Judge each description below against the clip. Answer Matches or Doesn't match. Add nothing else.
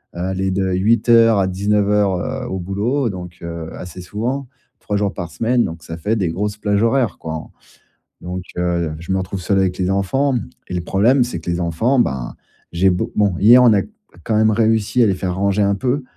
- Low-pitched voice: Matches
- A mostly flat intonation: Doesn't match